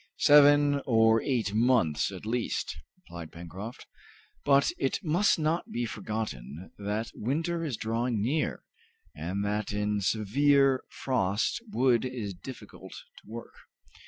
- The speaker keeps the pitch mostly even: No, average, 5.1 semitones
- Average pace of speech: No, slow, 125 wpm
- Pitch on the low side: Yes, low, 115 Hz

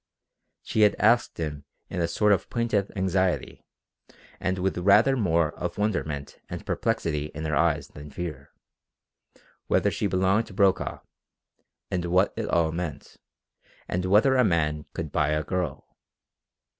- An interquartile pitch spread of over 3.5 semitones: Yes, average, 4.4 semitones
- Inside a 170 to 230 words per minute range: No, average, 145 wpm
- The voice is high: No, very low, 90 Hz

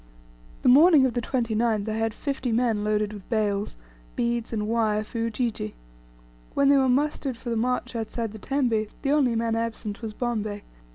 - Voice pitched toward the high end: Yes, high, 230 Hz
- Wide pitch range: No, narrow, 2.6 semitones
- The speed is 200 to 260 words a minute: No, average, 180 wpm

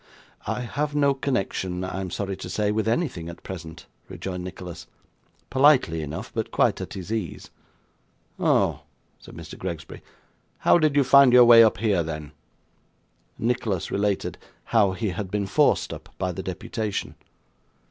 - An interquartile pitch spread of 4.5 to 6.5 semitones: Yes, average, 4.9 semitones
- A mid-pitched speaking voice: No, low, 100 Hz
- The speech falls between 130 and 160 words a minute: Yes, average, 155 wpm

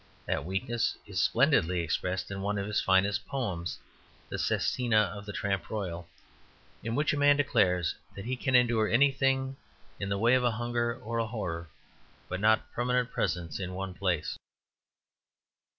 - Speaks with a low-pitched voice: Yes, low, 105 Hz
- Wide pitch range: No, average, 4.7 semitones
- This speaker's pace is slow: No, average, 155 wpm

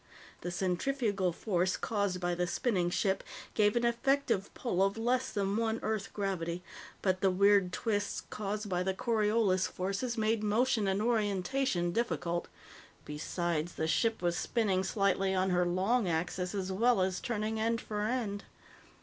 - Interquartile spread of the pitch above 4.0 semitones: No, average, 3.5 semitones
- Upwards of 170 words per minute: No, average, 155 wpm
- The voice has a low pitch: No, high, 200 Hz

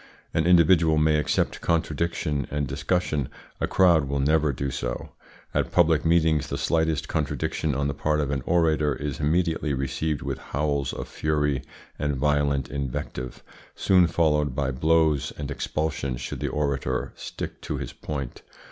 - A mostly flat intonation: Yes, narrow, 2.3 semitones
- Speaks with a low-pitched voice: Yes, very low, 75 Hz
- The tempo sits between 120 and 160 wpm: Yes, average, 155 wpm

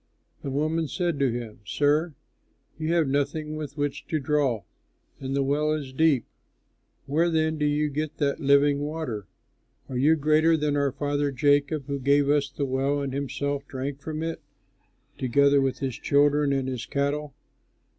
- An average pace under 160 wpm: No, average, 165 wpm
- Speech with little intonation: Yes, narrow, 1.7 semitones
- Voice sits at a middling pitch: Yes, medium, 145 Hz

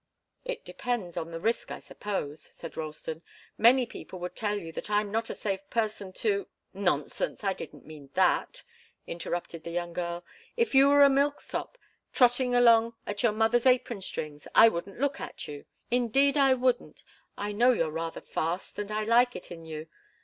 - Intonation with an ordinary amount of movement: No, wide, 6.3 semitones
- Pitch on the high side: Yes, high, 210 Hz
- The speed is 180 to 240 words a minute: Yes, average, 185 wpm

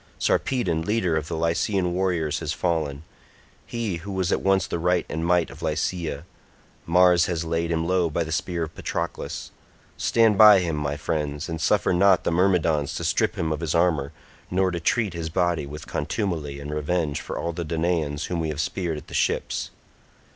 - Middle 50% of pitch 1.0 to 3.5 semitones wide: Yes, narrow, 2.5 semitones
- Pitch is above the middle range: No, very low, 85 Hz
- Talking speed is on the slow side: No, average, 190 wpm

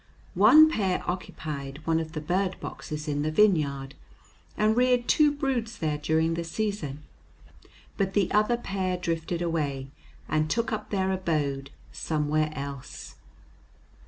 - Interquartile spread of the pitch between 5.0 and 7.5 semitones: Yes, wide, 5.4 semitones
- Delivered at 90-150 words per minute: Yes, slow, 135 wpm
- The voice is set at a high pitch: No, medium, 165 Hz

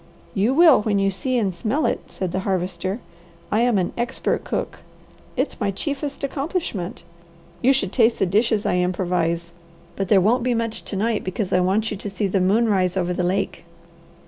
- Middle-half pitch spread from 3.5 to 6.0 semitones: Yes, average, 4.2 semitones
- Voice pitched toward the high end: Yes, high, 200 Hz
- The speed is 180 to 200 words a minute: Yes, average, 195 wpm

